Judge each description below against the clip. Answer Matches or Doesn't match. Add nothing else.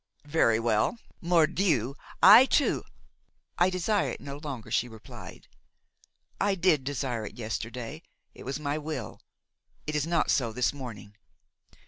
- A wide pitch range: Matches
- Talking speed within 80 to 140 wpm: Matches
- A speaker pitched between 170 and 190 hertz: Doesn't match